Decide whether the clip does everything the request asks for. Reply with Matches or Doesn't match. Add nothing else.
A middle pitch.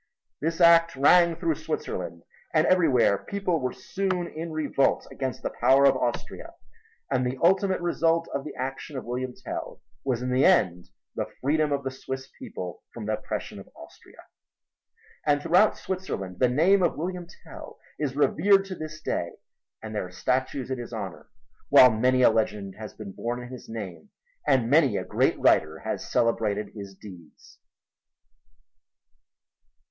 Doesn't match